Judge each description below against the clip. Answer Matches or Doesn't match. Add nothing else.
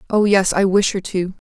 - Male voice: Doesn't match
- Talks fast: Matches